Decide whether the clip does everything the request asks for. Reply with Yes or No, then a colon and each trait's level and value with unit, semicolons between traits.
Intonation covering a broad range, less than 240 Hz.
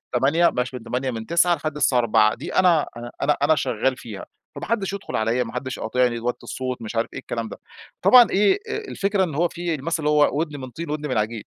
Yes: wide, 6.0 semitones; low, 135 Hz